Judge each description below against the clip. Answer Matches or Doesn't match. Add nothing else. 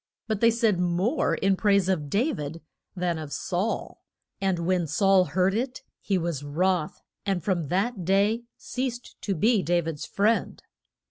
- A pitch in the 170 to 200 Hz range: Matches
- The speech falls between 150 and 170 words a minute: Matches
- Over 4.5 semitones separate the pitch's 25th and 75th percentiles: Doesn't match